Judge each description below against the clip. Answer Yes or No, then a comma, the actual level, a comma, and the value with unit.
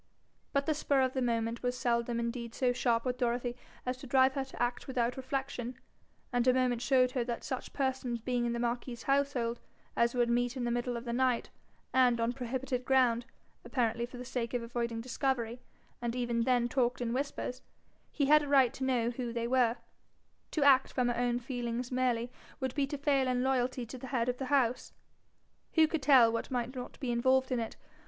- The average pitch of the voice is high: Yes, very high, 250 Hz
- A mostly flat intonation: Yes, narrow, 1.7 semitones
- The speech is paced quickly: Yes, fast, 210 wpm